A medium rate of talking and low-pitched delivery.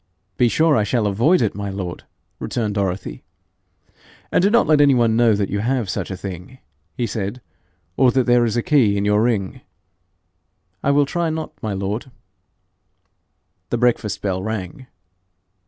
Yes: average, 165 wpm; low, 110 Hz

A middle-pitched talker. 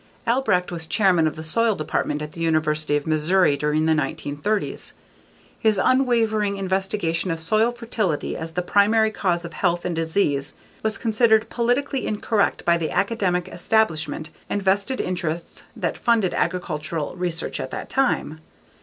Yes: medium, 180 Hz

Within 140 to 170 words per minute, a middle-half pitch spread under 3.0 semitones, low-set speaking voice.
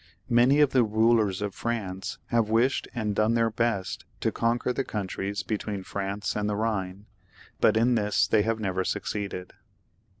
Yes: average, 165 wpm; narrow, 2.5 semitones; low, 110 Hz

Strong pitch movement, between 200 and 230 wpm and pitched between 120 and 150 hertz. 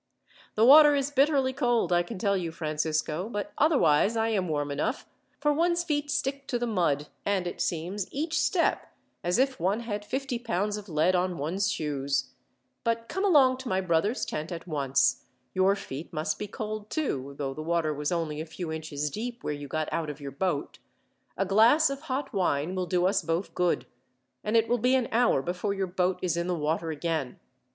No: wide, 7.3 semitones; fast, 205 wpm; medium, 185 Hz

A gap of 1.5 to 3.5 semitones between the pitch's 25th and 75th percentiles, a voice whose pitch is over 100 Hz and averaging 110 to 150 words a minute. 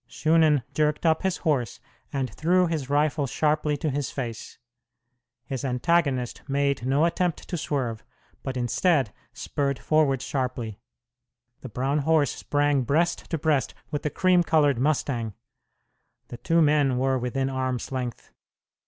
Yes: average, 3.2 semitones; medium, 140 Hz; average, 140 wpm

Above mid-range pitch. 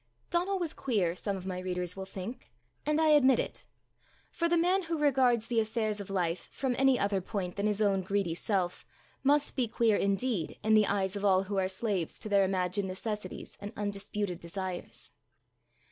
Yes: high, 205 Hz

